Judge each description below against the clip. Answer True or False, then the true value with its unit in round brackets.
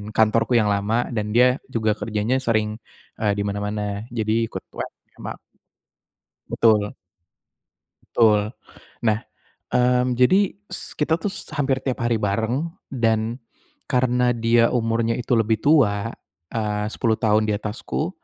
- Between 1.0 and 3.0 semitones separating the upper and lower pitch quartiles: True (2.6 semitones)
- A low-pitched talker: True (115 Hz)